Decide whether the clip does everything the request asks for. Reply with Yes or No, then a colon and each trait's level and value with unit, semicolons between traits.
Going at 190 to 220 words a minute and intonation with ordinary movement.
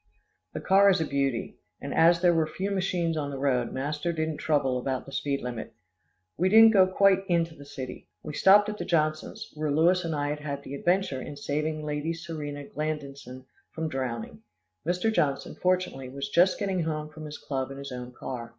Yes: average, 200 wpm; average, 3.8 semitones